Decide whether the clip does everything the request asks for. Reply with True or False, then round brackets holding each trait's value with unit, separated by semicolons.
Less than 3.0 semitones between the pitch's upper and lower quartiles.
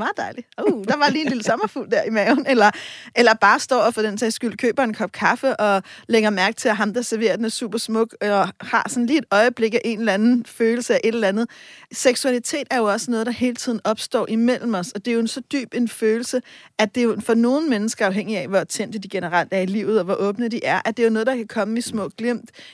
True (2.5 semitones)